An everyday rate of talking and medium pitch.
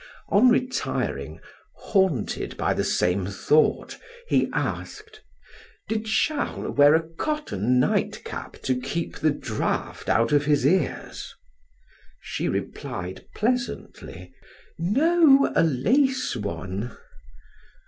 No: slow, 100 wpm; medium, 165 Hz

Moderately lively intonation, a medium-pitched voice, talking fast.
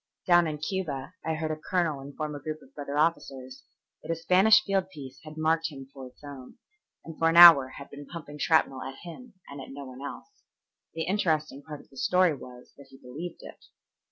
Yes: average, 3.4 semitones; medium, 155 Hz; fast, 215 wpm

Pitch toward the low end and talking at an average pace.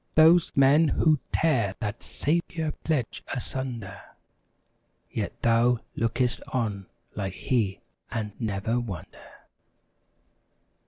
No: low, 120 Hz; slow, 105 wpm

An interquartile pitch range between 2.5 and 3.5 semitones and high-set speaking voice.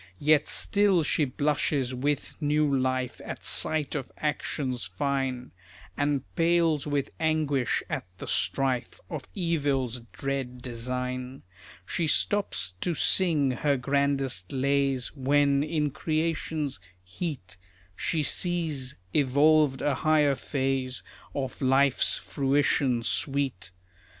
No: average, 2.8 semitones; medium, 140 Hz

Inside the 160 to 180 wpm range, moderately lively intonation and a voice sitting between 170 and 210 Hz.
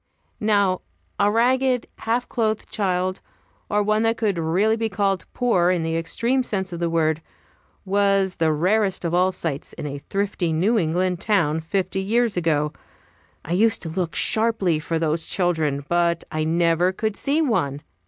Yes: average, 165 wpm; average, 4.6 semitones; medium, 185 Hz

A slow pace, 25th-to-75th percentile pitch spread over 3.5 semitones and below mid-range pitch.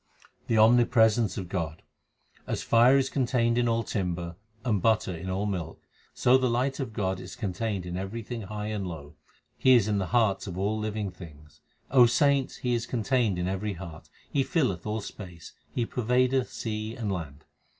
No: average, 180 wpm; average, 4.4 semitones; low, 110 Hz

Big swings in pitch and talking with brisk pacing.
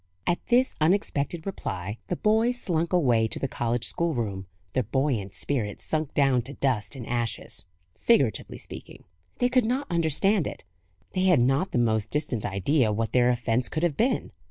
No: wide, 7.0 semitones; average, 170 wpm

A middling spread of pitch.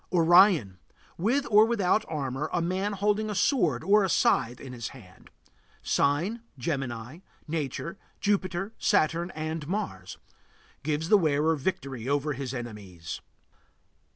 No: wide, 6.6 semitones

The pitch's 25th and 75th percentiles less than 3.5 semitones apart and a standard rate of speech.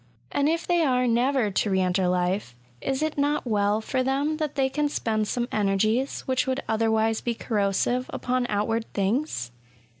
No: average, 4.5 semitones; average, 180 wpm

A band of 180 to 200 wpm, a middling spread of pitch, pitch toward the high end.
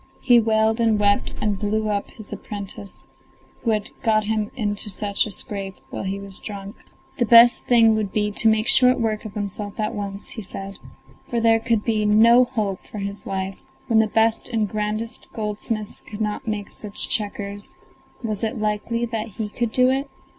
No: average, 190 wpm; narrow, 1.7 semitones; high, 215 Hz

